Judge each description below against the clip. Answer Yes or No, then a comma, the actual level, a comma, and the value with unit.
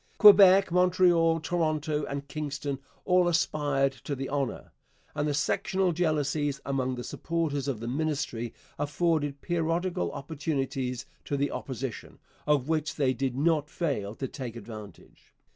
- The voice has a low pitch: No, medium, 145 Hz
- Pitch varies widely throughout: No, average, 3.4 semitones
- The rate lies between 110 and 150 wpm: Yes, slow, 135 wpm